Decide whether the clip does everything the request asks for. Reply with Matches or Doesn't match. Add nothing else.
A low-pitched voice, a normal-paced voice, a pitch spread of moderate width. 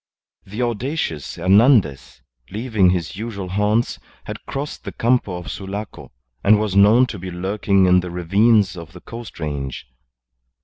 Matches